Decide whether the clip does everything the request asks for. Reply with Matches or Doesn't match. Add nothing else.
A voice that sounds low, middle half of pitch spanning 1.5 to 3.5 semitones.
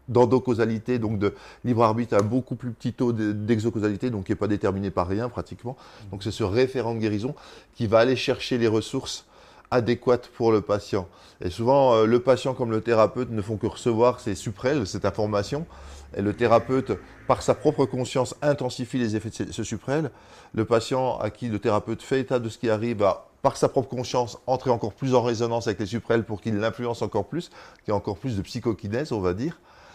Matches